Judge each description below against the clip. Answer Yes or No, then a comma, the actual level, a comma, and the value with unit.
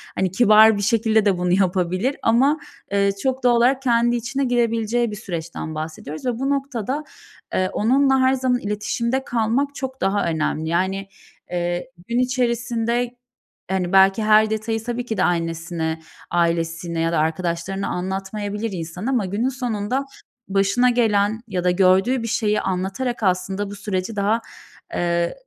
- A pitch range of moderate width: Yes, average, 4.8 semitones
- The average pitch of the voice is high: Yes, high, 210 Hz